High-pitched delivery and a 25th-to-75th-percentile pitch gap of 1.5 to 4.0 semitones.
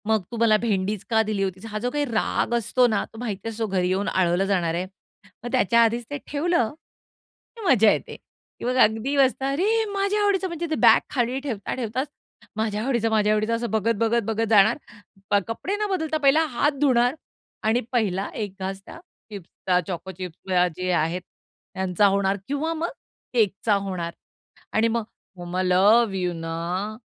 No: high, 220 Hz; average, 4.6 semitones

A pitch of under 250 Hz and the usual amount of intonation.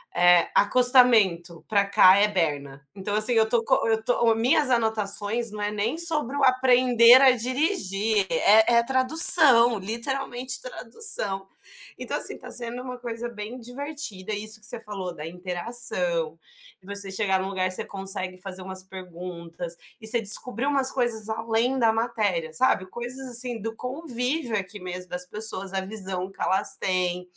Yes: high, 220 Hz; average, 4.5 semitones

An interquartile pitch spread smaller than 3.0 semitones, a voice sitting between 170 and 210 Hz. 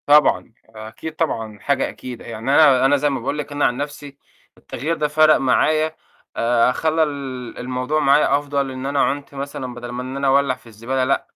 No: narrow, 2.6 semitones; low, 135 Hz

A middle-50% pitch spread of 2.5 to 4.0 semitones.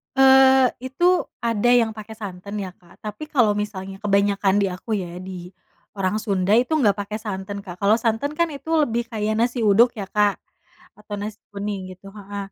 Yes: average, 2.9 semitones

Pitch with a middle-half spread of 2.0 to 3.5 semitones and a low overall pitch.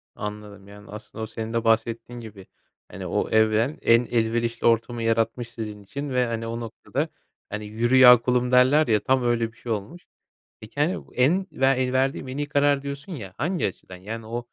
Yes: average, 2.9 semitones; low, 115 Hz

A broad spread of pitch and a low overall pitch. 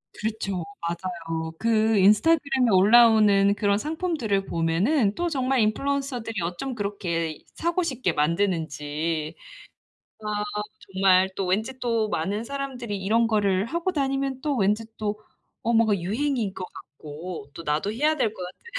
No: wide, 5.7 semitones; high, 210 Hz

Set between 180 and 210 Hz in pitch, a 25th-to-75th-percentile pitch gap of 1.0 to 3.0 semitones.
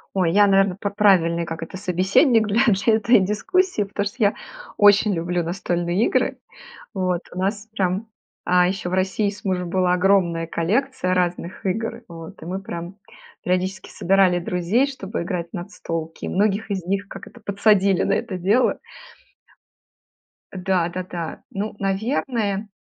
Yes: high, 190 Hz; narrow, 2.5 semitones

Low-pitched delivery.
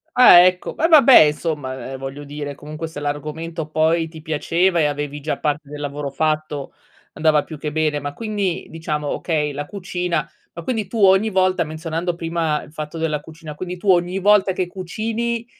No: medium, 160 Hz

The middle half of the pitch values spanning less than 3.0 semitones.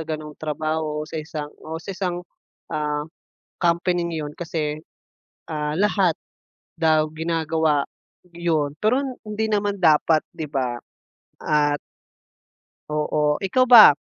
Yes: narrow, 2.4 semitones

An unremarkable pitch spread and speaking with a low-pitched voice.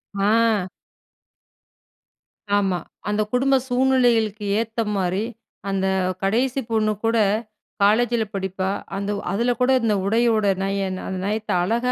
No: average, 3.2 semitones; high, 215 Hz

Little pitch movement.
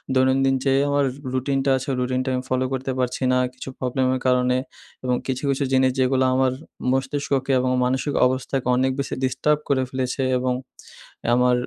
Yes: narrow, 0.9 semitones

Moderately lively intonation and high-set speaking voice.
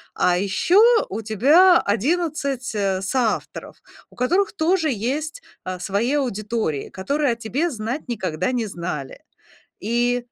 No: wide, 6.6 semitones; high, 240 Hz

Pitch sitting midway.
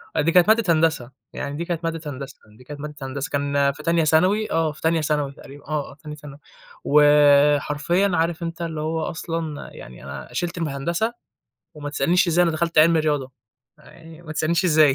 Yes: medium, 155 Hz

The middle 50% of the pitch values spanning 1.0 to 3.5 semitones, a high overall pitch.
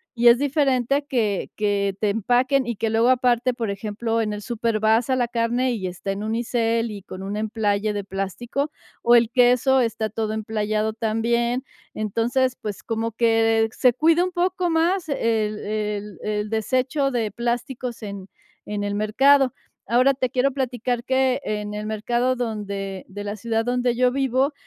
Yes: average, 3.1 semitones; high, 230 Hz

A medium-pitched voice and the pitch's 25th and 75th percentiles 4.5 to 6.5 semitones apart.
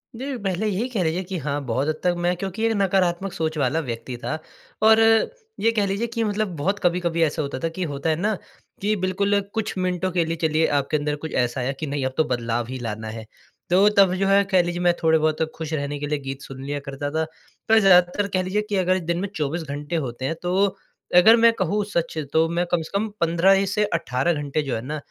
Yes: medium, 170 Hz; average, 5.1 semitones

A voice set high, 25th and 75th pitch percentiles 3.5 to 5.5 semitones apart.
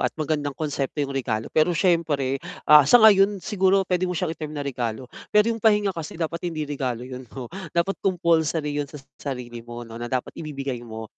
No: medium, 150 Hz; average, 5.2 semitones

